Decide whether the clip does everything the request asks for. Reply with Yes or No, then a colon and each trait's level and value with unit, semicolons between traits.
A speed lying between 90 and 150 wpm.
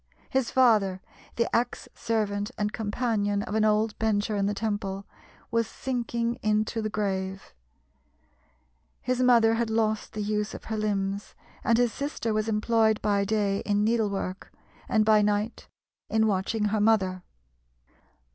Yes: average, 145 wpm